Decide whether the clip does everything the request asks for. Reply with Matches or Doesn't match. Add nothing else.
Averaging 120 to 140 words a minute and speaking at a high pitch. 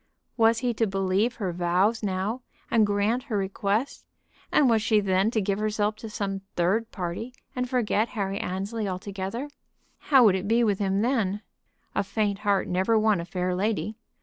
Doesn't match